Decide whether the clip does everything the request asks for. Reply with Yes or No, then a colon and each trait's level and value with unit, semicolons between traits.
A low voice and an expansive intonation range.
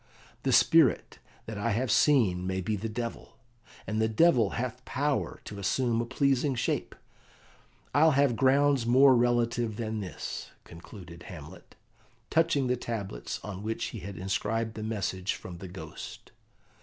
No: low, 115 Hz; average, 4.6 semitones